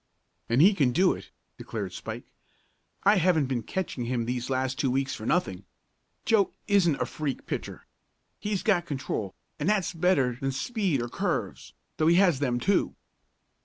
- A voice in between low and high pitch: Yes, medium, 145 Hz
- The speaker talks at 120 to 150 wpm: No, average, 165 wpm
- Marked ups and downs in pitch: Yes, wide, 6.6 semitones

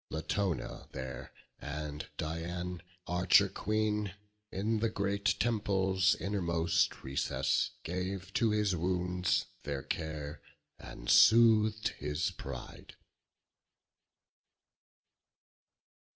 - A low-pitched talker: Yes, very low, 90 Hz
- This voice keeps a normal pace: No, slow, 80 wpm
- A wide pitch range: No, average, 4.5 semitones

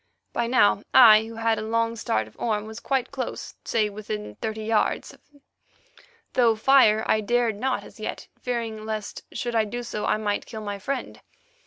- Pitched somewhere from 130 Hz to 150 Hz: No, high, 220 Hz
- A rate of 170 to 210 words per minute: Yes, average, 180 wpm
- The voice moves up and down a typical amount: No, narrow, 1.9 semitones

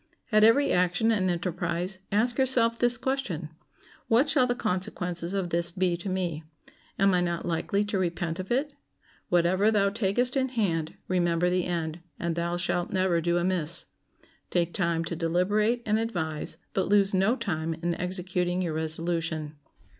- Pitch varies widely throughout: No, average, 3.6 semitones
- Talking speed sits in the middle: Yes, average, 160 wpm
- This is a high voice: No, medium, 180 Hz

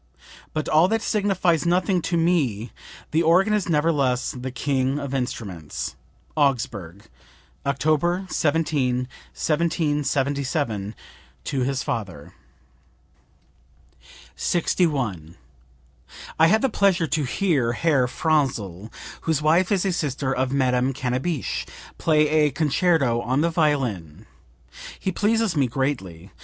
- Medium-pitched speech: Yes, medium, 145 Hz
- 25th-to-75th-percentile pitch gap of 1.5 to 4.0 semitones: No, average, 5.0 semitones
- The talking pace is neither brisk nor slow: No, slow, 115 wpm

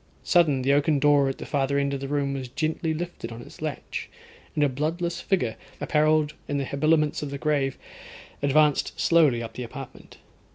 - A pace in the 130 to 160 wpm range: No, average, 190 wpm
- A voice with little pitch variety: Yes, narrow, 2.2 semitones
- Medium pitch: Yes, medium, 145 Hz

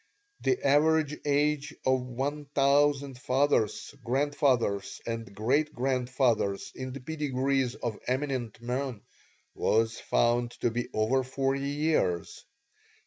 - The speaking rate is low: Yes, slow, 110 wpm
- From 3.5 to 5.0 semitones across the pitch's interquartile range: No, average, 3.1 semitones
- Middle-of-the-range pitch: No, low, 130 Hz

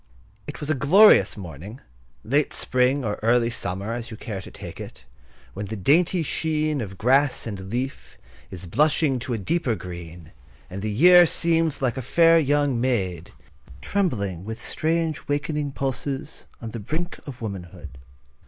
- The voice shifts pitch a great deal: Yes, wide, 6.9 semitones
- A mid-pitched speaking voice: No, low, 125 Hz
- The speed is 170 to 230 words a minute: No, average, 160 wpm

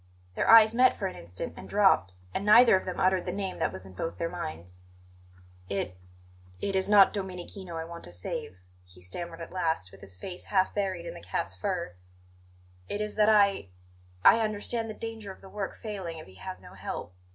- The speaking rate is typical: No, fast, 210 wpm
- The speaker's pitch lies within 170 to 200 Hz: Yes, medium, 185 Hz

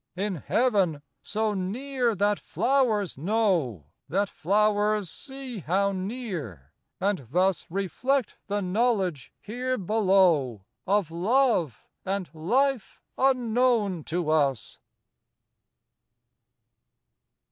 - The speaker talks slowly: Yes, slow, 90 wpm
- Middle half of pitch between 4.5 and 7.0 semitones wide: Yes, average, 5.0 semitones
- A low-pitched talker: No, high, 200 Hz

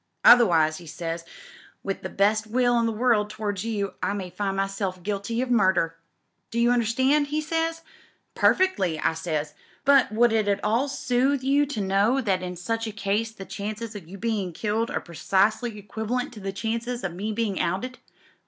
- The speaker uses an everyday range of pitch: Yes, average, 3.8 semitones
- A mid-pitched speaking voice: No, high, 215 Hz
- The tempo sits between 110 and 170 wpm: No, average, 185 wpm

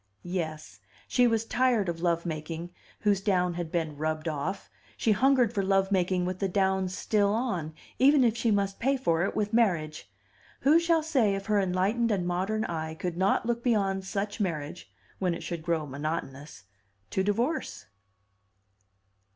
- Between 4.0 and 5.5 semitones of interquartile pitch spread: Yes, average, 4.5 semitones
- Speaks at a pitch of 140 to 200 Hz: Yes, high, 190 Hz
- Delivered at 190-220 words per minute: No, average, 165 wpm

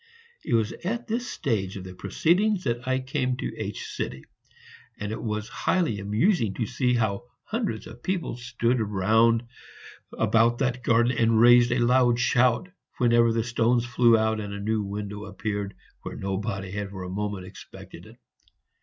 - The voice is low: Yes, low, 115 Hz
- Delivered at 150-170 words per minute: Yes, average, 165 wpm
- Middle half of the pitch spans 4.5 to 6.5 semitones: No, average, 3.2 semitones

